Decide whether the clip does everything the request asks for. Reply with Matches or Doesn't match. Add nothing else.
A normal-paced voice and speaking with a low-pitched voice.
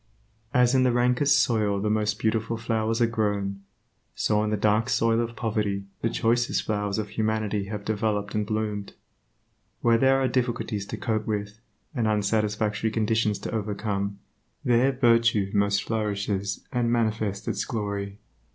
Matches